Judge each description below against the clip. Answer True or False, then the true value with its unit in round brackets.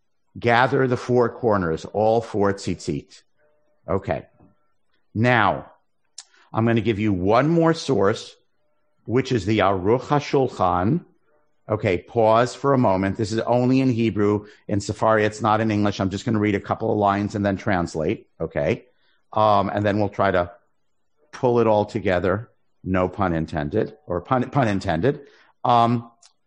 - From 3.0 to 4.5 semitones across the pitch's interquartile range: True (3.5 semitones)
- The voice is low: True (110 Hz)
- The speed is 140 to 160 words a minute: True (155 wpm)